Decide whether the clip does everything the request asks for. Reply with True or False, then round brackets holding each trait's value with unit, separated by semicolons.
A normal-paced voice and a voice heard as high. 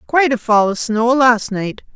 False (215 wpm; 235 Hz)